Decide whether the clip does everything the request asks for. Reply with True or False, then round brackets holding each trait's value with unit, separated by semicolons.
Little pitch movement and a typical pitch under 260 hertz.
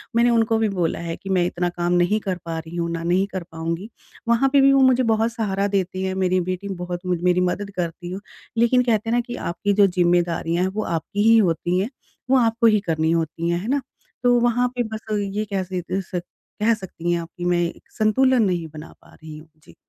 False (4.4 semitones; 185 Hz)